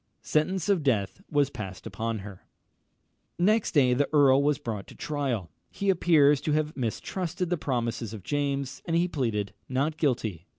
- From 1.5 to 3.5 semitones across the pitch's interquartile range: No, wide, 5.4 semitones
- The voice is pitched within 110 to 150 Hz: Yes, medium, 140 Hz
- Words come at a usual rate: Yes, average, 165 wpm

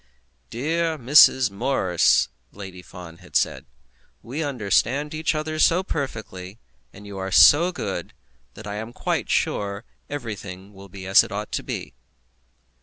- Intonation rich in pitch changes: Yes, wide, 7.1 semitones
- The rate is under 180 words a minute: Yes, average, 145 wpm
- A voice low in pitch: Yes, low, 105 Hz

